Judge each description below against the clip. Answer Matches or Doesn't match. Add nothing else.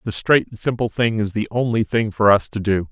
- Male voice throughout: Matches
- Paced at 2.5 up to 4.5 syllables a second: Doesn't match